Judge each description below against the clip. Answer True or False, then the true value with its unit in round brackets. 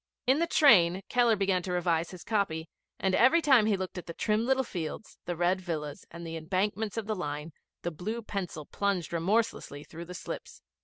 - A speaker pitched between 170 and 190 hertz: True (185 Hz)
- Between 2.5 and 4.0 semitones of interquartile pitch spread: False (4.4 semitones)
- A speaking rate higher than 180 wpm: True (205 wpm)